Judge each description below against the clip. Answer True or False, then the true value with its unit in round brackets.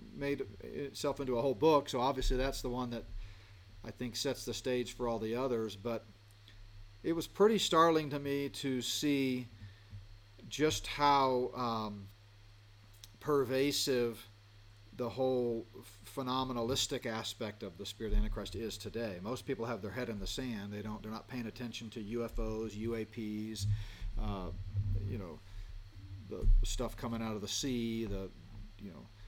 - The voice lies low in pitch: True (110 Hz)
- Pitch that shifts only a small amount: False (3.5 semitones)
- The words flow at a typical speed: True (155 wpm)